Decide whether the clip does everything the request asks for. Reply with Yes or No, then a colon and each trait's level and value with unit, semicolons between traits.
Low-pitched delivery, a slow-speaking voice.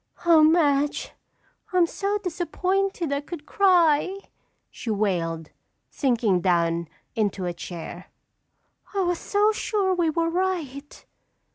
No: very high, 315 Hz; slow, 115 wpm